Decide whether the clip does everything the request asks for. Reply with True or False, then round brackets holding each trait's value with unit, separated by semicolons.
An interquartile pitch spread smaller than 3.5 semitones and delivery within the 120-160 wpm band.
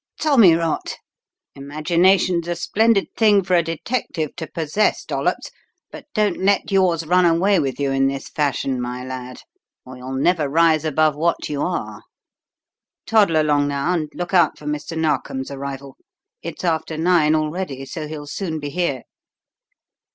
False (3.9 semitones; 155 wpm)